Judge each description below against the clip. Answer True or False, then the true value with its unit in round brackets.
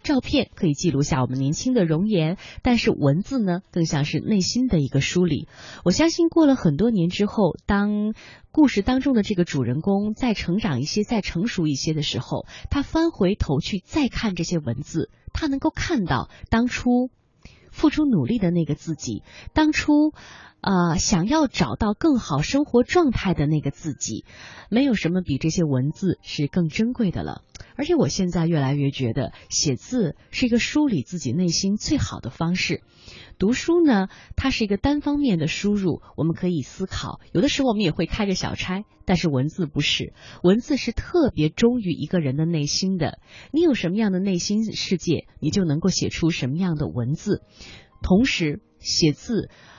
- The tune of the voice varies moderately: False (7.4 semitones)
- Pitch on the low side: False (185 Hz)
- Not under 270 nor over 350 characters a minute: True (275 characters per minute)